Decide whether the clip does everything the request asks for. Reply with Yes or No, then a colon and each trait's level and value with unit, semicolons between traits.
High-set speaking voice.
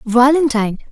Yes: very high, 250 Hz